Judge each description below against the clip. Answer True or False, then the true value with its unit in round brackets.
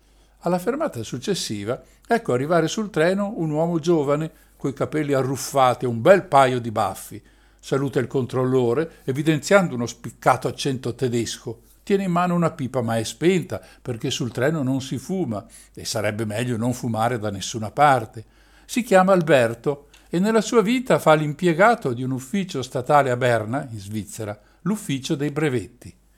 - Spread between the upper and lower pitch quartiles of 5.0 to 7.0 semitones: True (5.6 semitones)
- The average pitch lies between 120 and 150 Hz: True (135 Hz)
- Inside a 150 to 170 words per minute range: True (160 wpm)